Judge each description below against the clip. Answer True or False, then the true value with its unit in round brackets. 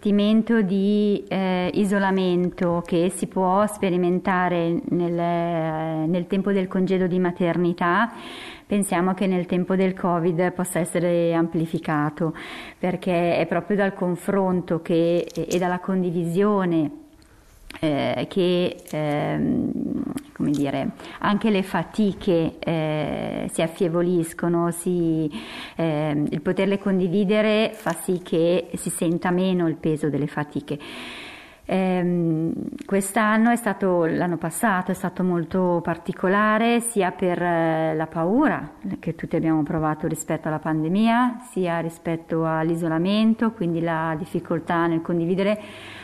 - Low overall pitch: False (180 Hz)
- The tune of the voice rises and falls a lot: False (3.0 semitones)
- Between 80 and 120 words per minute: True (115 wpm)